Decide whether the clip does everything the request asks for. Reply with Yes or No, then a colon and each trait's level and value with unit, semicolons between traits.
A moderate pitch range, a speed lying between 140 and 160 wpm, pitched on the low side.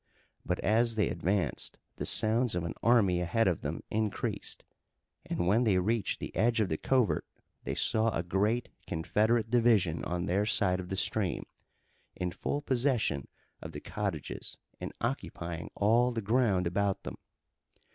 Yes: average, 4.3 semitones; average, 155 wpm; low, 105 Hz